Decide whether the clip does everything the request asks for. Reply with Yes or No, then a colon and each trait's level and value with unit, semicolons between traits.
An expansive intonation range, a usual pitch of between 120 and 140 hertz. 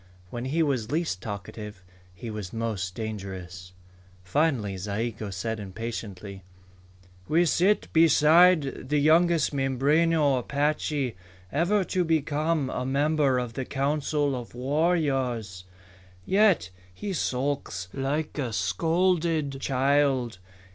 Yes: wide, 5.9 semitones; low, 135 Hz